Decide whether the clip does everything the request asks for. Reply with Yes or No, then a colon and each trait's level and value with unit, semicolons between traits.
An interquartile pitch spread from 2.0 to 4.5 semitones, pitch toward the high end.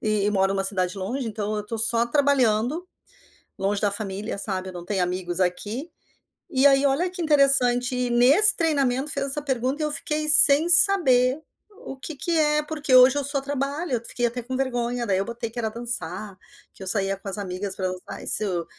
No: wide, 5.6 semitones; high, 245 Hz